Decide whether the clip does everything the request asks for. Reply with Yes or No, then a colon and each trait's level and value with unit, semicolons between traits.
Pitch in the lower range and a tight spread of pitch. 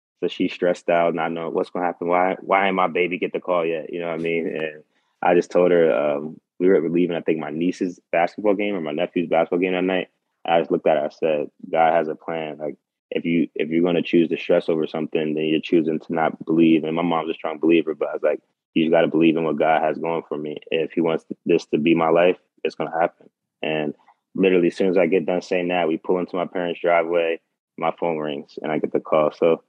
Yes: very low, 85 Hz; narrow, 2.0 semitones